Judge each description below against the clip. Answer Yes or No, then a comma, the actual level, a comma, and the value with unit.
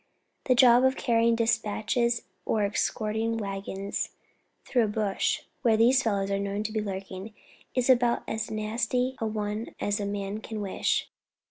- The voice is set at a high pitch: Yes, high, 220 Hz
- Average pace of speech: Yes, average, 155 wpm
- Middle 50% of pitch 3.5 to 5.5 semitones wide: No, narrow, 2.4 semitones